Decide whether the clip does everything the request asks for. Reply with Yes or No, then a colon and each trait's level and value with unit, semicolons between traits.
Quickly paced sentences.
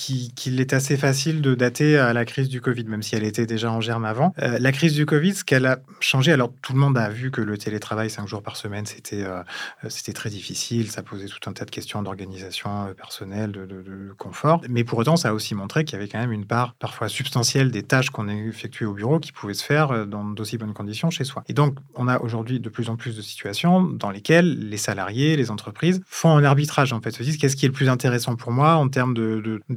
Yes: fast, 260 wpm